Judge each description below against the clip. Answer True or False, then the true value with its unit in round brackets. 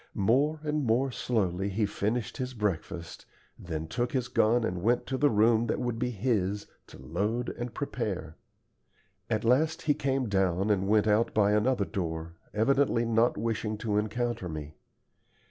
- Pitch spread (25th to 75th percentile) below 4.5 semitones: True (3.9 semitones)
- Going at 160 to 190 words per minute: True (165 wpm)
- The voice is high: False (110 Hz)